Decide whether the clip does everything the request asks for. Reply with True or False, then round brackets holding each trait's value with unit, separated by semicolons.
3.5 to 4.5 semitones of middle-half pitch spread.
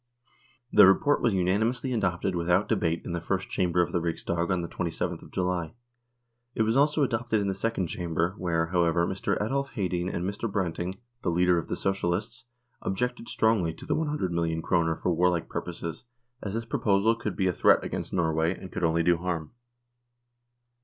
True (4.2 semitones)